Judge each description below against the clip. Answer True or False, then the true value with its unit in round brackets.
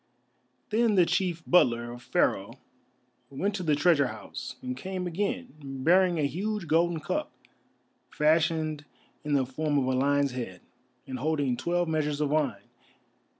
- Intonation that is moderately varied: True (4.5 semitones)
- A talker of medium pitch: True (155 Hz)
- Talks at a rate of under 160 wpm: True (150 wpm)